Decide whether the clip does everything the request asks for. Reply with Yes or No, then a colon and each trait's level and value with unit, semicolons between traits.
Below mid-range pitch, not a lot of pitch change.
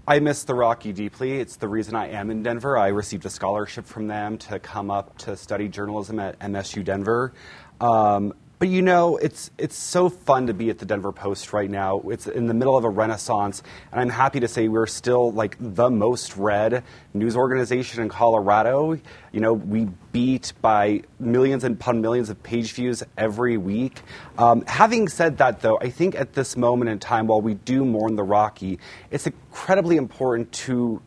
No: low, 115 Hz; average, 3.6 semitones